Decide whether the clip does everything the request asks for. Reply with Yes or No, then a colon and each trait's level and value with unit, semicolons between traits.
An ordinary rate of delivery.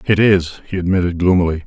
Yes: average, 180 wpm